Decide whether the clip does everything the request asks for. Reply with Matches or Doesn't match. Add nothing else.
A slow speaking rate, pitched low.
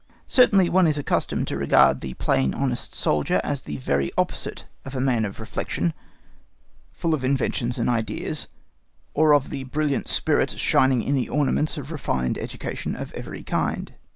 Doesn't match